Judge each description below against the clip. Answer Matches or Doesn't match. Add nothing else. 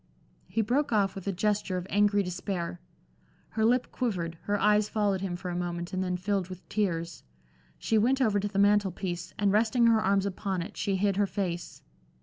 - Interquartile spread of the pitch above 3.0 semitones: Doesn't match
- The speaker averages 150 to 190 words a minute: Doesn't match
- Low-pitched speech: Doesn't match